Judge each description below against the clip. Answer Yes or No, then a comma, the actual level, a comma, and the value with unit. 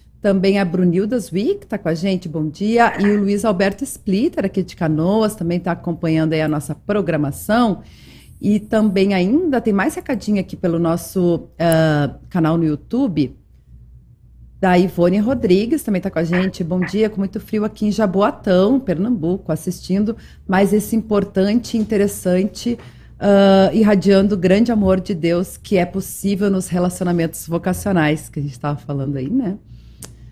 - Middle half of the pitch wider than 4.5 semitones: No, average, 3.8 semitones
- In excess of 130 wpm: Yes, average, 160 wpm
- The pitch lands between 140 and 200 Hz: Yes, high, 190 Hz